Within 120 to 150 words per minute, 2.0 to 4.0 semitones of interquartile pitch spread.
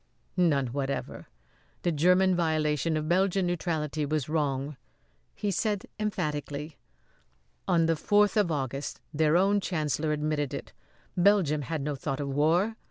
Yes: slow, 135 wpm; average, 3.5 semitones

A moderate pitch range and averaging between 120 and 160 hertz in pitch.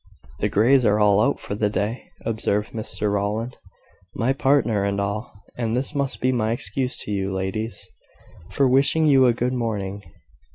No: average, 3.7 semitones; low, 110 Hz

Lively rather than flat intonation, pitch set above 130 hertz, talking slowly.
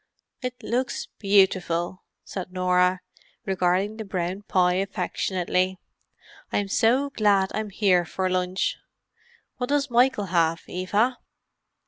No: average, 3.0 semitones; high, 190 Hz; slow, 110 wpm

